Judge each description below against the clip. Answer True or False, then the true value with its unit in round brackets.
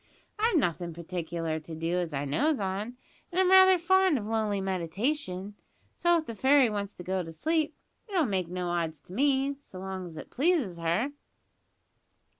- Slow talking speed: False (175 wpm)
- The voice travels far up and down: True (8.9 semitones)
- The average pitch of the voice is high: True (200 Hz)